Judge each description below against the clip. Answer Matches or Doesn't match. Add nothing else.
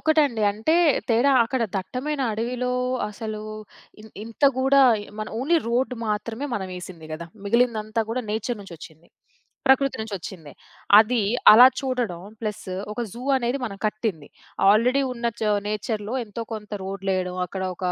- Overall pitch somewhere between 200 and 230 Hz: Matches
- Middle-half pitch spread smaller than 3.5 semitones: Doesn't match